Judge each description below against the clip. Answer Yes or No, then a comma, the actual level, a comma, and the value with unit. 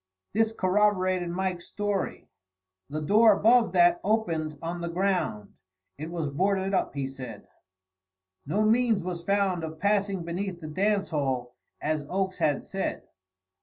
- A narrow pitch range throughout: No, average, 4.4 semitones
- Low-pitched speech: No, medium, 185 Hz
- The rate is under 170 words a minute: Yes, average, 140 wpm